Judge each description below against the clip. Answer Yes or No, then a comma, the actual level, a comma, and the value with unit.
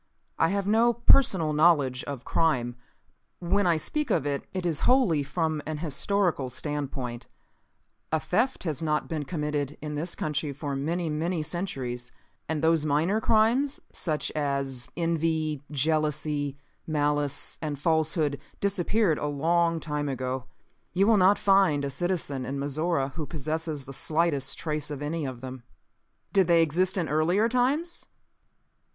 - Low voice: No, medium, 155 Hz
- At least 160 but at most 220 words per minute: No, average, 145 wpm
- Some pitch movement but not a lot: Yes, average, 3.5 semitones